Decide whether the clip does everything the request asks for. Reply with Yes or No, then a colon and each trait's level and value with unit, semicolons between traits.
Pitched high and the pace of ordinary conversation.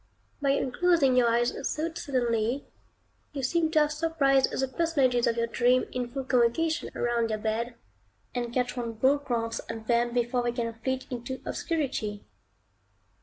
Yes: very high, 250 Hz; average, 160 wpm